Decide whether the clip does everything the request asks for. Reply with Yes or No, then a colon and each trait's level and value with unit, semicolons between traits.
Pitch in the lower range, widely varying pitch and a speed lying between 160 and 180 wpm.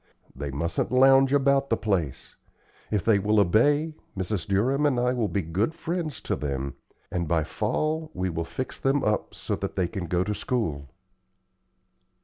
Yes: low, 105 Hz; wide, 7.7 semitones; average, 170 wpm